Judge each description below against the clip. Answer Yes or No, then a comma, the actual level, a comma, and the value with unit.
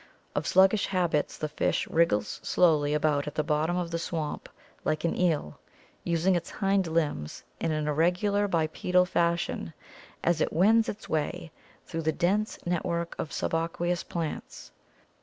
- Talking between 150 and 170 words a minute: Yes, average, 155 wpm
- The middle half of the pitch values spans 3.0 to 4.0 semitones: No, narrow, 2.6 semitones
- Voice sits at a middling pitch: Yes, medium, 170 Hz